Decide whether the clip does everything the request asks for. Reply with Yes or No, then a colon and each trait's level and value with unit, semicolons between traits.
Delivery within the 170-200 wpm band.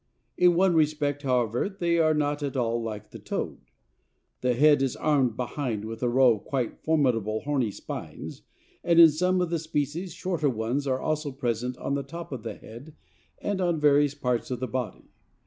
Yes: average, 190 wpm